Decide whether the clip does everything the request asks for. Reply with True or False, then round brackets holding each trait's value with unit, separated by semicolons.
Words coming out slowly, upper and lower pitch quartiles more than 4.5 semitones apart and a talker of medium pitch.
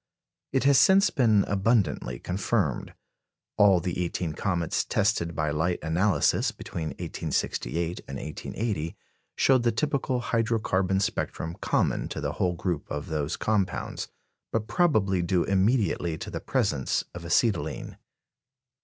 False (130 wpm; 5.2 semitones; 95 Hz)